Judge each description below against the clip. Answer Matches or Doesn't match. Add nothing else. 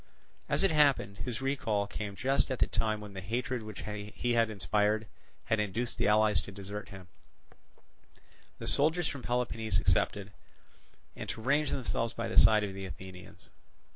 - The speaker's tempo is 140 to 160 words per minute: Doesn't match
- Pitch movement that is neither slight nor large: Matches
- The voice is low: Matches